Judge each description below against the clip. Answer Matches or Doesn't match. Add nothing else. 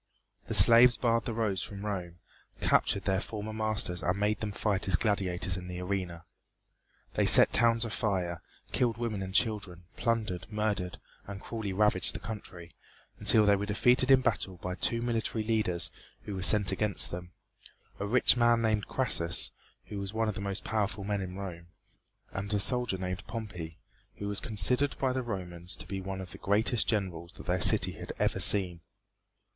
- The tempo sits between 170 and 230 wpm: Matches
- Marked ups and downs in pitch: Doesn't match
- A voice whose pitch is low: Matches